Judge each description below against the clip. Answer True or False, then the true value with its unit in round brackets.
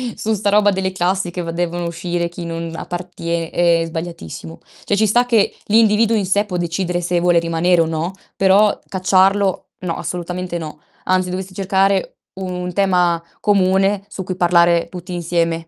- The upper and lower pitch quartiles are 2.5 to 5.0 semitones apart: False (2.1 semitones)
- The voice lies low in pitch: False (180 Hz)